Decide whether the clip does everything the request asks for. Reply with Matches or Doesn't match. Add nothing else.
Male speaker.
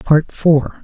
Matches